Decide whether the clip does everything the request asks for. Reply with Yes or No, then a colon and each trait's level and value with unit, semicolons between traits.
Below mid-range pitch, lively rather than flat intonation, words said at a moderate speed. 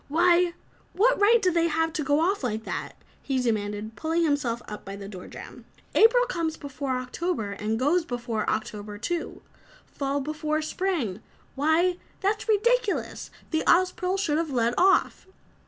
No: very high, 310 Hz; wide, 7.3 semitones; average, 155 wpm